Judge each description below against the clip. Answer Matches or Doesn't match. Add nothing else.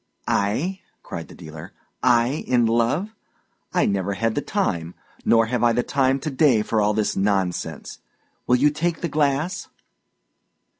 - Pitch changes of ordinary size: Doesn't match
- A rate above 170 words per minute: Doesn't match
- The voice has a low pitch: Matches